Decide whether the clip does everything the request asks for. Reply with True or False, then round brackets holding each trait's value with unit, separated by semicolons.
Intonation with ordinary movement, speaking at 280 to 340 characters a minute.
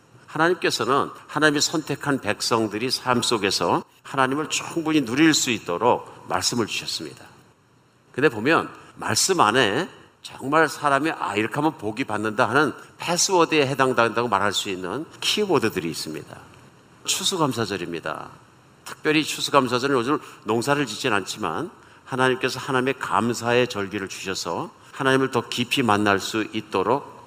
True (4.7 semitones; 330 characters per minute)